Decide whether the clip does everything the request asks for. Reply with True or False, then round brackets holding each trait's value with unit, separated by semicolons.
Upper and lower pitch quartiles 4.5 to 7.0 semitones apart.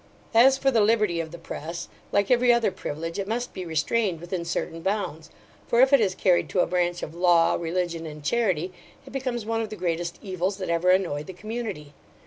True (4.9 semitones)